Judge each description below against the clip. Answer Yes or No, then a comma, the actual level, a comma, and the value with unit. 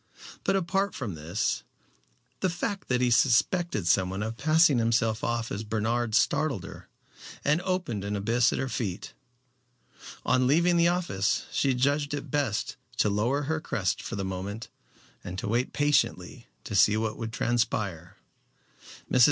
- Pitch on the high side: No, low, 120 Hz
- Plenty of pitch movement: Yes, wide, 6.0 semitones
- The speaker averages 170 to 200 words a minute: No, average, 155 wpm